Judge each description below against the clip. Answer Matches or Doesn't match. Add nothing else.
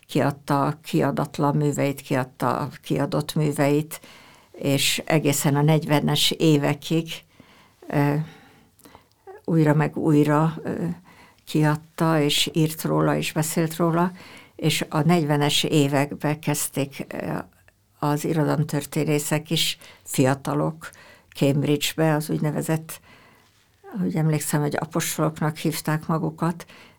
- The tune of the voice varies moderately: Doesn't match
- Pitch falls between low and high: Matches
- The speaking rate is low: Matches